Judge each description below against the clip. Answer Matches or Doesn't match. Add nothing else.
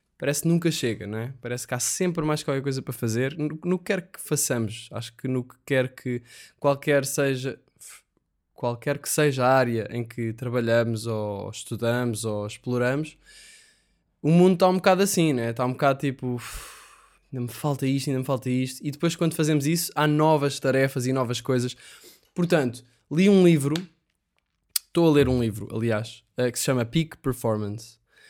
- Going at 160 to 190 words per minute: Matches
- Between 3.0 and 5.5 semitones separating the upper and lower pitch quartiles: Matches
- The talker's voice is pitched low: Matches